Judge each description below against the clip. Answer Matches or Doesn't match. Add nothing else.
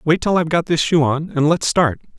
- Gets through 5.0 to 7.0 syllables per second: Matches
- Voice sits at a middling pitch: Matches